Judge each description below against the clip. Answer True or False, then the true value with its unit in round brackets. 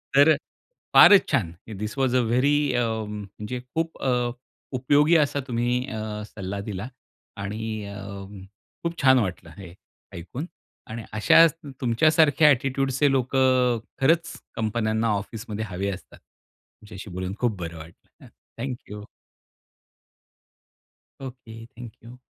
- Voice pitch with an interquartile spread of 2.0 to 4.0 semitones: False (4.4 semitones)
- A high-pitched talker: False (120 Hz)